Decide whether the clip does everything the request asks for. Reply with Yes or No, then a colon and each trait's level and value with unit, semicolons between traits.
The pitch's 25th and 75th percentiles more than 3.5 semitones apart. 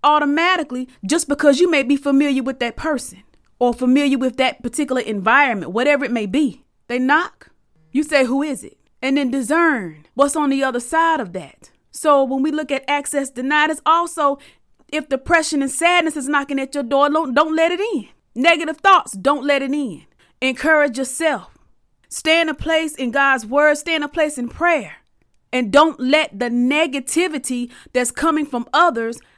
No: average, 3.2 semitones